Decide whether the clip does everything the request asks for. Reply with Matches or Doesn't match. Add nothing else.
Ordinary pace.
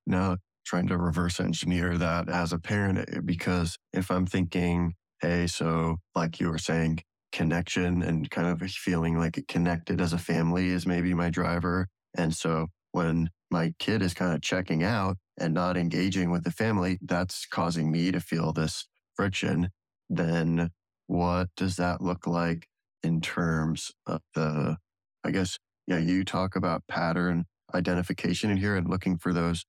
Matches